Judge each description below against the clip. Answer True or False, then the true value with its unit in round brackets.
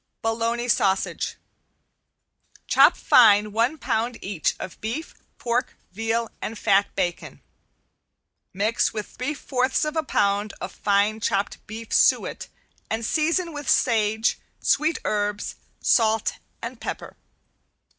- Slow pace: True (115 wpm)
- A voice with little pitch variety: False (3.2 semitones)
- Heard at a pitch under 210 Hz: False (225 Hz)